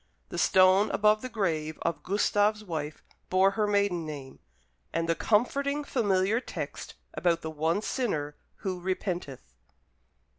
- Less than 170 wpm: Yes, slow, 135 wpm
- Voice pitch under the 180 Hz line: No, medium, 185 Hz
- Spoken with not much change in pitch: No, average, 4.6 semitones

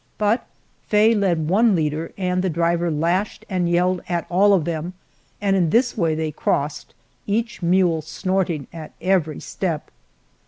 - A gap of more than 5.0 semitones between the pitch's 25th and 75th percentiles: No, average, 3.1 semitones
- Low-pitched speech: No, medium, 175 Hz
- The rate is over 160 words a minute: No, average, 155 wpm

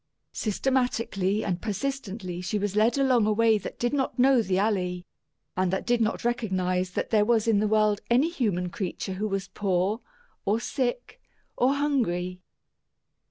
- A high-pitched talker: Yes, high, 215 Hz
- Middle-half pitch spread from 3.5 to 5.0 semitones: Yes, average, 4.4 semitones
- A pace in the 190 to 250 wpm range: No, average, 160 wpm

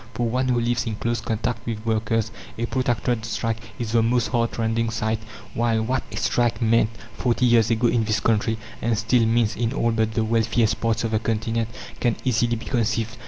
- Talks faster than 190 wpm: Yes, average, 200 wpm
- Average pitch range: No, narrow, 1.1 semitones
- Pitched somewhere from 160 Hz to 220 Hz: No, low, 115 Hz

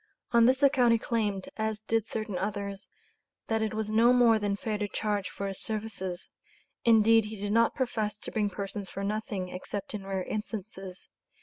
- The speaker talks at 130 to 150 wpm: No, average, 185 wpm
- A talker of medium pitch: No, high, 210 Hz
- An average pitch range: No, narrow, 2.1 semitones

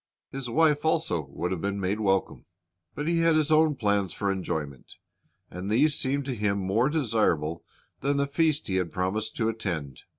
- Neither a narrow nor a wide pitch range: No, wide, 7.3 semitones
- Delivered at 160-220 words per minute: Yes, average, 185 wpm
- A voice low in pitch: Yes, low, 110 Hz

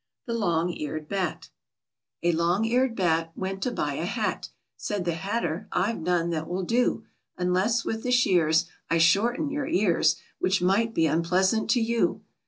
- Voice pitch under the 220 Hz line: Yes, medium, 185 Hz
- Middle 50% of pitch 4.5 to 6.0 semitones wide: Yes, average, 5.2 semitones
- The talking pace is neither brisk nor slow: Yes, average, 170 wpm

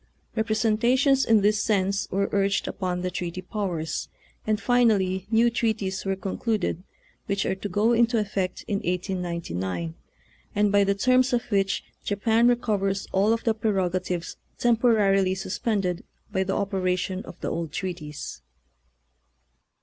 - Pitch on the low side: No, high, 200 Hz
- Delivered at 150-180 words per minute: No, slow, 135 wpm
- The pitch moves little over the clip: No, average, 3.0 semitones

